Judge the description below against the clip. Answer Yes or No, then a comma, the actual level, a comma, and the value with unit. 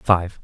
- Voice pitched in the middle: No, very low, 90 Hz